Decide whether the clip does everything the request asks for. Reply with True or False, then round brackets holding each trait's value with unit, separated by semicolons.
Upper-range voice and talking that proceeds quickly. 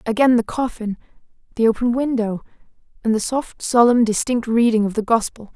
False (230 Hz; 160 wpm)